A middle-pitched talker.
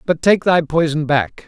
Yes: medium, 155 Hz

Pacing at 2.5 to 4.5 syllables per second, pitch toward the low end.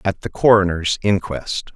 Yes: 4.4 syllables/s; very low, 95 Hz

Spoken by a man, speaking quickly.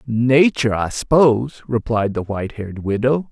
No: male; average, 145 wpm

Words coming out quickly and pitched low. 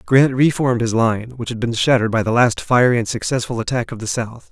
Yes: fast, 240 wpm; low, 120 Hz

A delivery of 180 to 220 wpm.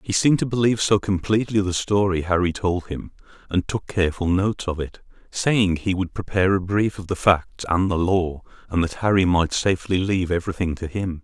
Yes: fast, 205 wpm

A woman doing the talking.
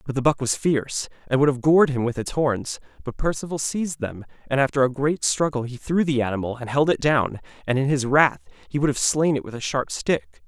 No: male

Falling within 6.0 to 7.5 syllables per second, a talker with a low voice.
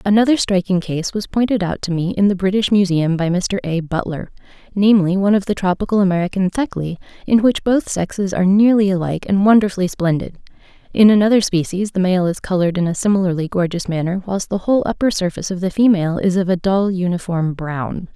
No: 6.1 syllables/s; high, 190 Hz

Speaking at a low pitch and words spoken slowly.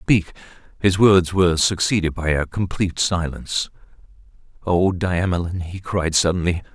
Yes: very low, 90 Hz; slow, 125 wpm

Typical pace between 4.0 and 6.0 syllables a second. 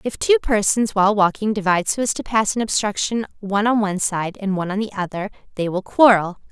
No: 6.2 syllables/s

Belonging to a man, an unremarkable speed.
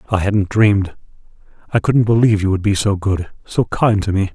Yes: male; average, 195 wpm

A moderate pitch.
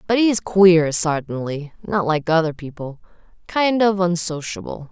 Yes: medium, 175 Hz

